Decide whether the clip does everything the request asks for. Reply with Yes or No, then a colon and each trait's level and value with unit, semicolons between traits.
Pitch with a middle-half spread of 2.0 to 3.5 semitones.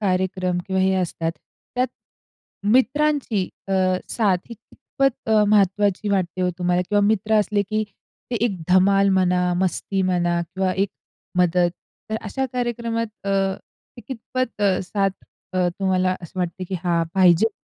Yes: average, 3.1 semitones